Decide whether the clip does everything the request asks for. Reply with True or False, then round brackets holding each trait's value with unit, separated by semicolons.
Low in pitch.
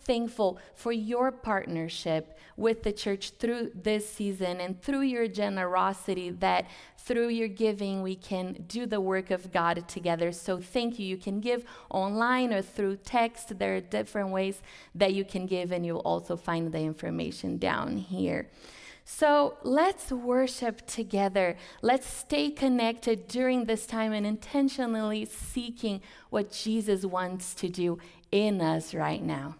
False (205 Hz)